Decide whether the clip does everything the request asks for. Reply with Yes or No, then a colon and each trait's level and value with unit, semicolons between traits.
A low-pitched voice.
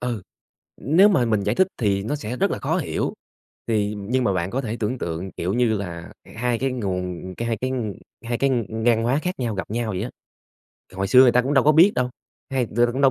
Yes: low, 115 Hz